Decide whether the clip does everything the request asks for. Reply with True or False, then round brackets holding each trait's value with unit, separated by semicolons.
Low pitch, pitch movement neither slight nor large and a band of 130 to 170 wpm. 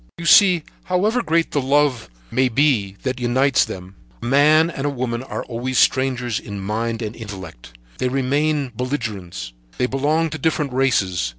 True (130 Hz; 4.4 semitones; 165 wpm)